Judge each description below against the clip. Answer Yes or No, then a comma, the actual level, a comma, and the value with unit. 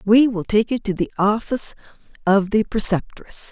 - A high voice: Yes, high, 210 Hz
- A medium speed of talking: Yes, average, 170 wpm